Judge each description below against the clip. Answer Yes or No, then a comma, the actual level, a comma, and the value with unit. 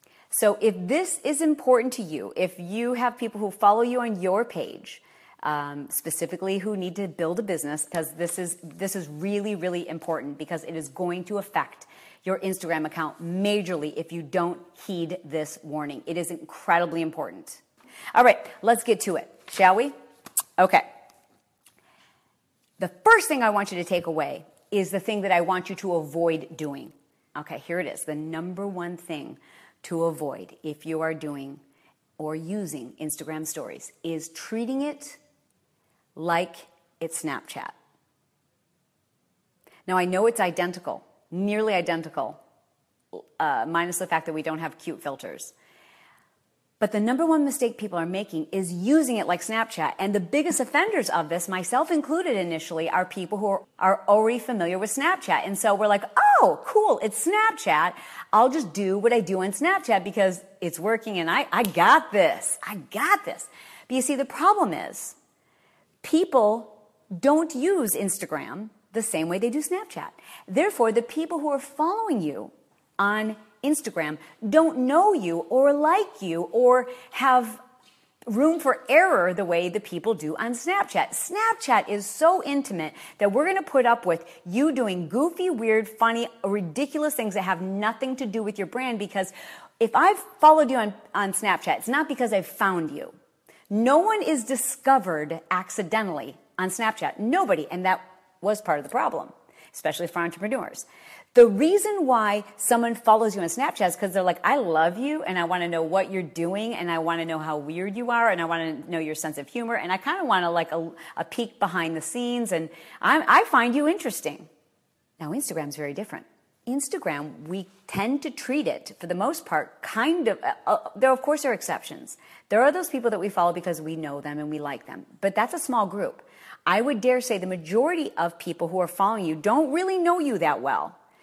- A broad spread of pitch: Yes, wide, 6.9 semitones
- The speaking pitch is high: Yes, high, 200 Hz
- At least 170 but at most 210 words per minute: Yes, average, 185 wpm